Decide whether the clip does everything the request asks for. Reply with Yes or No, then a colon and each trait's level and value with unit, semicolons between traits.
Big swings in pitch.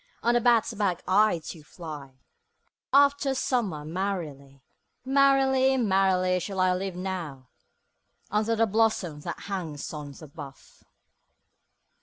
Yes: wide, 6.4 semitones